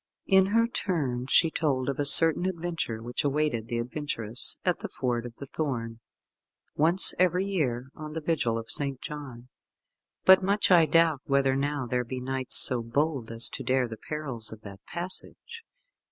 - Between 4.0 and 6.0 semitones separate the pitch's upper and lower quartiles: Yes, average, 5.2 semitones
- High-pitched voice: No, medium, 140 Hz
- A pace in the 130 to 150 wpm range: No, average, 175 wpm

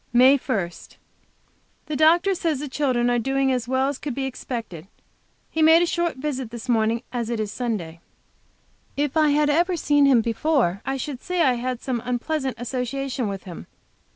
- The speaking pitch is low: No, very high, 260 Hz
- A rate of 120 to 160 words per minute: No, average, 180 wpm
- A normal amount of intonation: Yes, average, 3.7 semitones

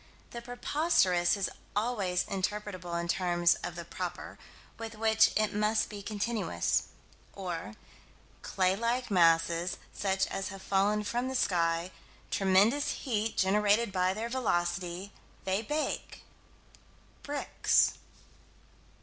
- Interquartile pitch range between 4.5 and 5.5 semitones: No, average, 3.7 semitones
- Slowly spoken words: Yes, slow, 115 wpm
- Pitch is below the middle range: No, high, 200 Hz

